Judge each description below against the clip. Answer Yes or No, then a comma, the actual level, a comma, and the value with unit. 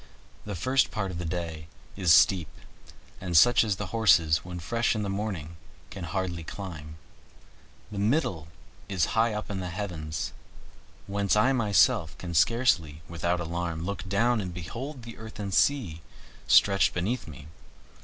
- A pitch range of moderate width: Yes, average, 4.2 semitones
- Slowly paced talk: No, average, 155 wpm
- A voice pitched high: No, very low, 95 Hz